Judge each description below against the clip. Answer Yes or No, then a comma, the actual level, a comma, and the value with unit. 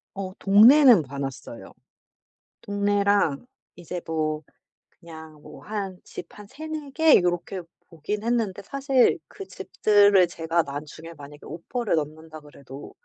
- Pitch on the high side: No, medium, 180 Hz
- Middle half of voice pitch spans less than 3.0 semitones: No, average, 5.2 semitones